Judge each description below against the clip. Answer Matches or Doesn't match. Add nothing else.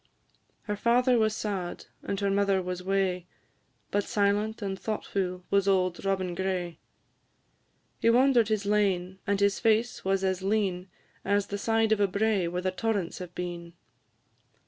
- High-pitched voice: Matches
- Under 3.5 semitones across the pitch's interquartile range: Matches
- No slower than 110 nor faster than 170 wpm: Matches